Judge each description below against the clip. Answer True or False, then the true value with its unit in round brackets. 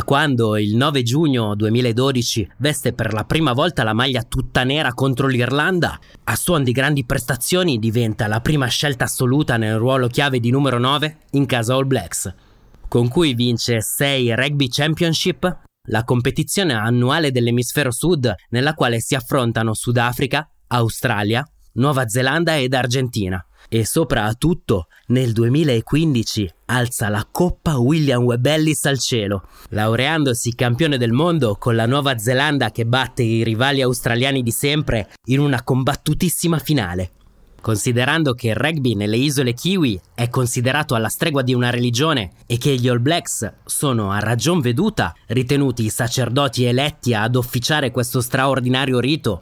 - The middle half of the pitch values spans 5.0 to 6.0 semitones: False (3.5 semitones)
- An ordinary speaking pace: True (145 wpm)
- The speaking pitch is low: True (125 Hz)